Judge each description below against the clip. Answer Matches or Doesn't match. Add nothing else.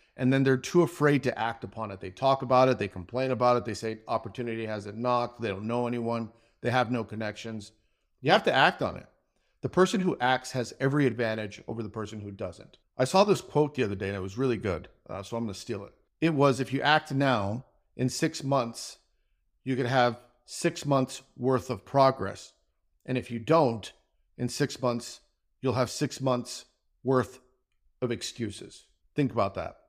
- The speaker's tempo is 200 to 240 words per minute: Matches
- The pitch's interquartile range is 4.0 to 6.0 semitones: Doesn't match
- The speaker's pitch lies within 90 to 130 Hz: Matches